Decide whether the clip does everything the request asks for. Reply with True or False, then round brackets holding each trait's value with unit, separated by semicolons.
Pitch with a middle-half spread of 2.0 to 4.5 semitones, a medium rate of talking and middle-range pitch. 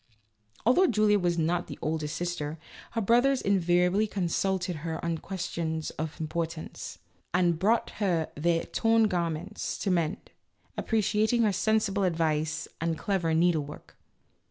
False (4.1 semitones; 130 wpm; 175 Hz)